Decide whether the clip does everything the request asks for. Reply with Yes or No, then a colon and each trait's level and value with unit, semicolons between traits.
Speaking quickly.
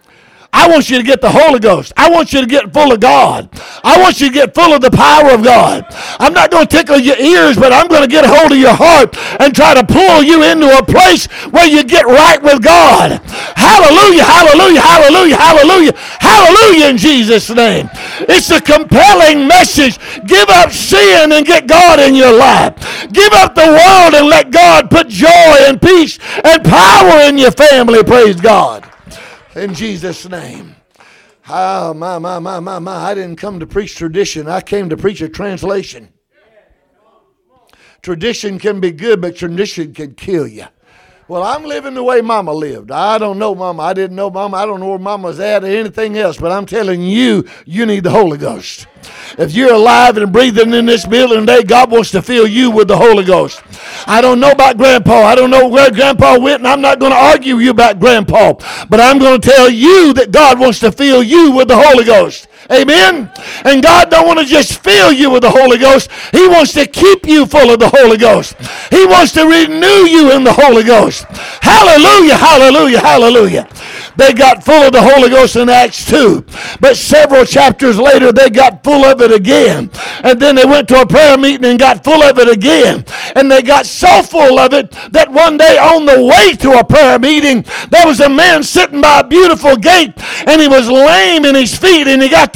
Yes: fast, 210 wpm